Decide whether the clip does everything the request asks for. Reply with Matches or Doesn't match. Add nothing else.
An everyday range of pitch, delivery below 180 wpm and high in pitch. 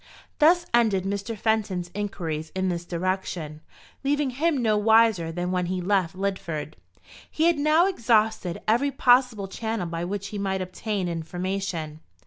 Matches